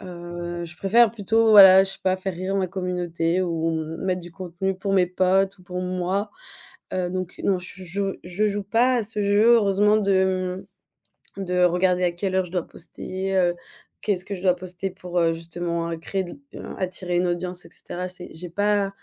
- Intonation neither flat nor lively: No, narrow, 1.7 semitones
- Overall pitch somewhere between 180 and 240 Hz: Yes, medium, 185 Hz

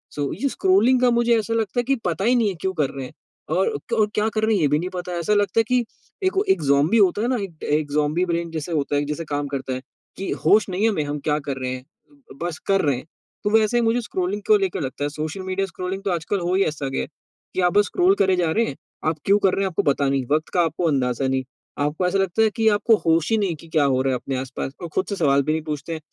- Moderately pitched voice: Yes, medium, 175 Hz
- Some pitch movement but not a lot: No, wide, 5.9 semitones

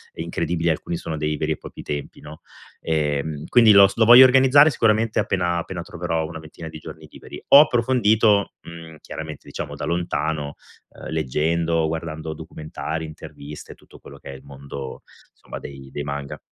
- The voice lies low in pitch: Yes, very low, 80 Hz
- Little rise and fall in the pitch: No, average, 3.8 semitones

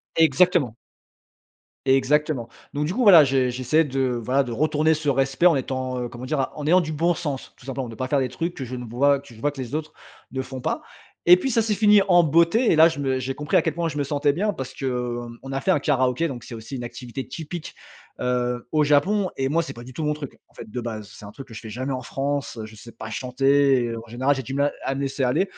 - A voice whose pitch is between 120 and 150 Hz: Yes, low, 135 Hz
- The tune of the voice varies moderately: Yes, average, 3.6 semitones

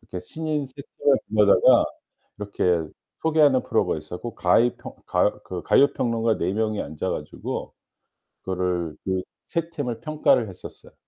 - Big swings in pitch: Yes, wide, 7.4 semitones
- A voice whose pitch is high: No, low, 115 Hz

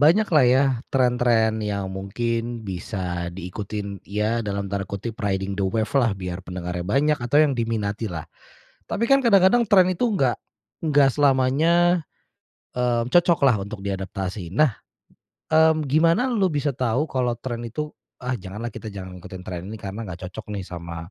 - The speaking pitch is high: No, low, 115 Hz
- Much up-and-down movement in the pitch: Yes, wide, 6.8 semitones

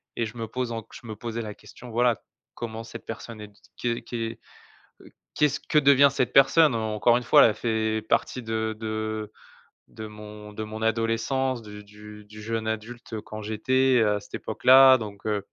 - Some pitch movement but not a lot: No, narrow, 2.0 semitones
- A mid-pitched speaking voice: No, low, 110 Hz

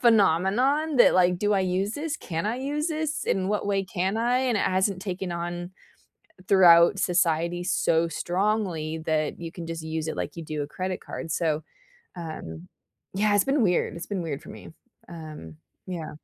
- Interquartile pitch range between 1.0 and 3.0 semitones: No, average, 4.0 semitones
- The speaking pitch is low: No, medium, 180 Hz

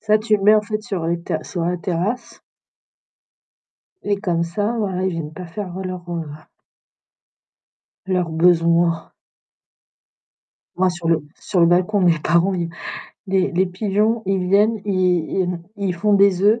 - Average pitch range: Yes, average, 3.1 semitones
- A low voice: No, medium, 185 Hz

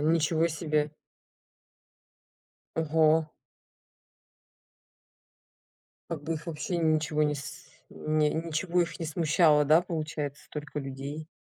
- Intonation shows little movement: Yes, narrow, 1.5 semitones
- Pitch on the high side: No, medium, 155 Hz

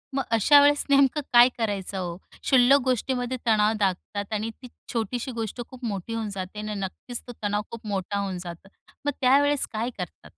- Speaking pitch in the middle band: No, high, 225 Hz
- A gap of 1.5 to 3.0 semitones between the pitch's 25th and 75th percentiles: No, average, 4.1 semitones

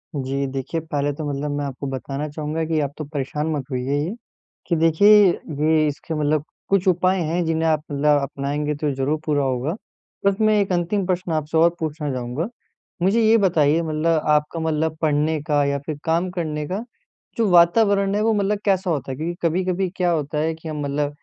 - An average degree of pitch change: Yes, average, 3.3 semitones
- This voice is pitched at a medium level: Yes, medium, 155 Hz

